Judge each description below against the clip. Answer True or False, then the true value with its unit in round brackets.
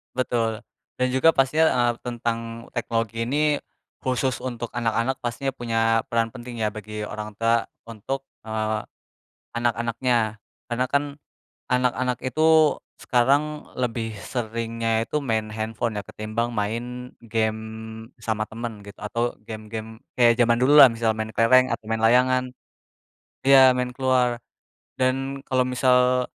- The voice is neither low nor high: False (120 Hz)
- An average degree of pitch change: False (2.2 semitones)